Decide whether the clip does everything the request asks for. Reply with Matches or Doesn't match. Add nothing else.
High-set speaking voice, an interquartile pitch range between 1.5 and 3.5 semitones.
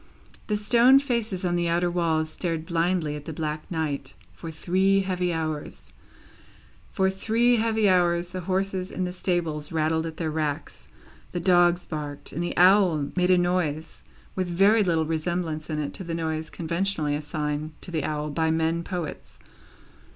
Doesn't match